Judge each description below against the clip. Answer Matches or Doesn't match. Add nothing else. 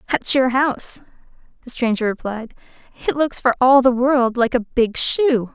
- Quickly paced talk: Doesn't match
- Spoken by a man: Doesn't match